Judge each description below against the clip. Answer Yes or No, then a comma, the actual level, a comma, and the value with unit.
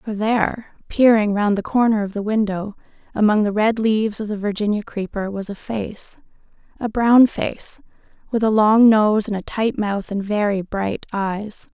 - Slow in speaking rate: No, average, 180 wpm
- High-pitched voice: Yes, high, 210 Hz